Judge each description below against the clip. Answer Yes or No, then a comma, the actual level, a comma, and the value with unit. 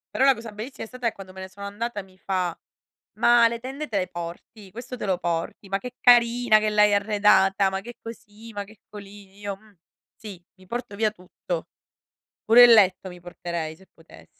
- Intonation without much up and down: No, average, 3.4 semitones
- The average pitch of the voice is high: Yes, high, 205 Hz